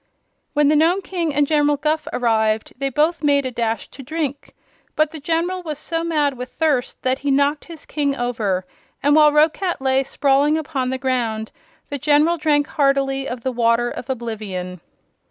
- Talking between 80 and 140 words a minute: No, average, 180 wpm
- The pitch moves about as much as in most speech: Yes, average, 3.5 semitones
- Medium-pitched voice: No, very high, 280 Hz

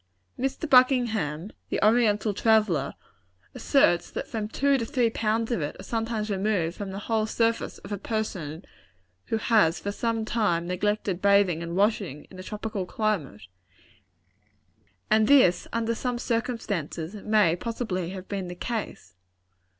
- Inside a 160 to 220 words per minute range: No, average, 145 wpm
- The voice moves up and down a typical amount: Yes, average, 4.0 semitones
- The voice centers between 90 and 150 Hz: No, high, 210 Hz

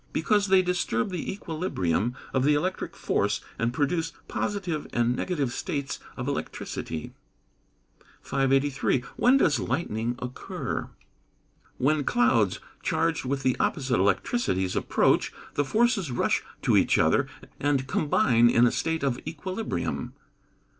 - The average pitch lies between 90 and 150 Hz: Yes, medium, 140 Hz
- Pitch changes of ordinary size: No, wide, 6.1 semitones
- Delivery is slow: Yes, slow, 125 wpm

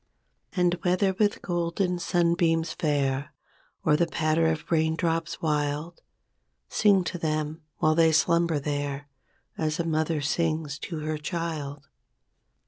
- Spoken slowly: Yes, slow, 125 wpm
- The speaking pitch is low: No, medium, 160 Hz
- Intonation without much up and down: Yes, narrow, 2.1 semitones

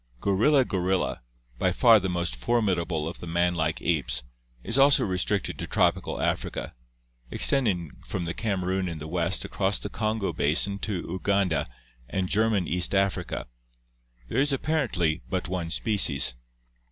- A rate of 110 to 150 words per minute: Yes, average, 145 wpm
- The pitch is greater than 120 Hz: No, very low, 95 Hz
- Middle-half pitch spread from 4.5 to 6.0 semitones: No, average, 3.5 semitones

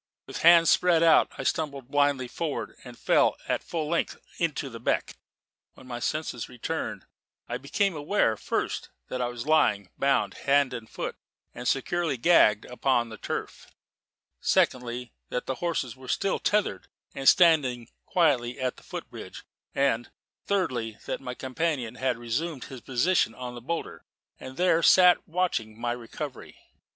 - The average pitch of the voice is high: No, low, 130 Hz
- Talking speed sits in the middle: Yes, average, 155 wpm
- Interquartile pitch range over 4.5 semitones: Yes, average, 5.0 semitones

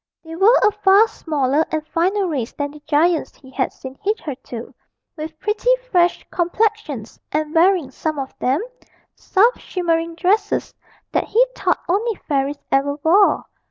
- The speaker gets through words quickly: No, average, 150 wpm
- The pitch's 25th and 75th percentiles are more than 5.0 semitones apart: Yes, wide, 5.5 semitones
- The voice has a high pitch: Yes, very high, 330 Hz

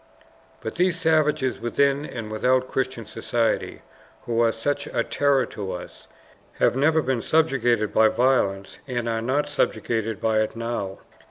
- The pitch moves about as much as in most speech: Yes, average, 3.7 semitones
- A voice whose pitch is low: Yes, low, 120 Hz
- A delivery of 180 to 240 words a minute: No, average, 150 wpm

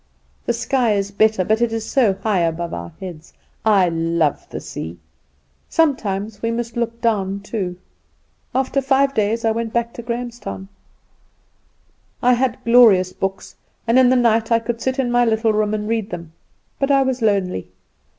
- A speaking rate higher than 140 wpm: Yes, average, 170 wpm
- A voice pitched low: No, high, 225 Hz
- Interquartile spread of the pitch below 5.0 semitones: Yes, average, 3.7 semitones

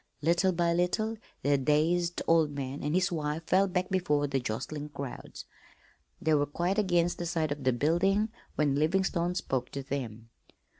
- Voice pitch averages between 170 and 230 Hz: No, medium, 160 Hz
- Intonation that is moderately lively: Yes, average, 3.7 semitones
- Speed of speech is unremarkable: Yes, average, 165 wpm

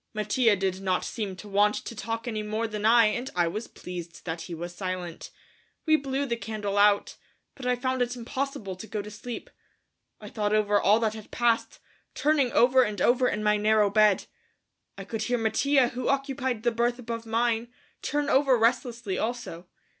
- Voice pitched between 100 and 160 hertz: No, high, 225 Hz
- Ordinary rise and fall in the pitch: Yes, average, 3.1 semitones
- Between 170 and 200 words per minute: Yes, average, 190 wpm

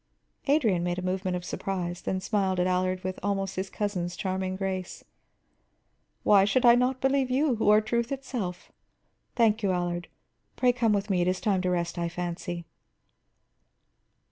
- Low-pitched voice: No, high, 190 Hz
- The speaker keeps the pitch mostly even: No, average, 3.6 semitones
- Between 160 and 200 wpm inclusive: Yes, average, 170 wpm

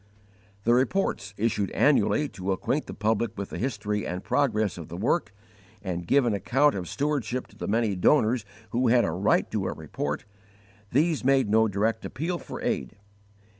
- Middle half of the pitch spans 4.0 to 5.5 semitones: Yes, average, 5.1 semitones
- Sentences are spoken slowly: No, average, 175 wpm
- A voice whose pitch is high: No, low, 110 Hz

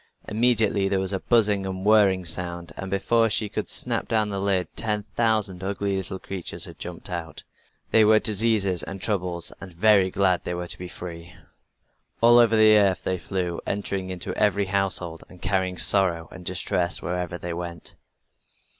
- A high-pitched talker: No, very low, 95 Hz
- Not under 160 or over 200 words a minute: Yes, average, 170 wpm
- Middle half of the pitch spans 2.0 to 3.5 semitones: Yes, average, 2.7 semitones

